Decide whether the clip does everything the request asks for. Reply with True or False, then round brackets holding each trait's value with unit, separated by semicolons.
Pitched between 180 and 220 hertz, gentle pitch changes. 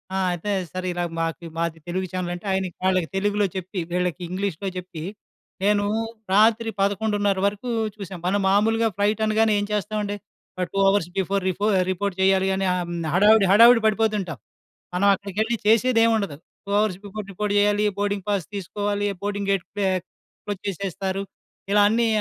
True (200 Hz; 2.1 semitones)